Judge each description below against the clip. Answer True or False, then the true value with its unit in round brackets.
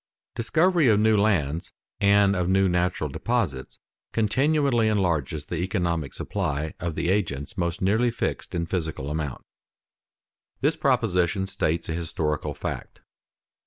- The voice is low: True (90 Hz)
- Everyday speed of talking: False (125 wpm)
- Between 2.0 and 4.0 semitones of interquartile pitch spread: False (5.3 semitones)